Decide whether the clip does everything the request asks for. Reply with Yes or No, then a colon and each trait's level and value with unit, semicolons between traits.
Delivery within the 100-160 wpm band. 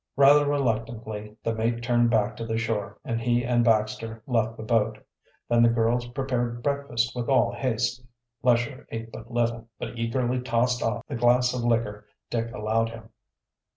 No: average, 170 wpm